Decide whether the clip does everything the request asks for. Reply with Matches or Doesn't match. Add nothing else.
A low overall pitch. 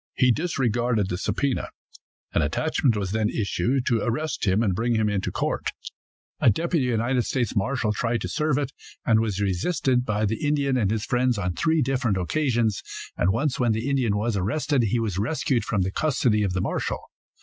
Matches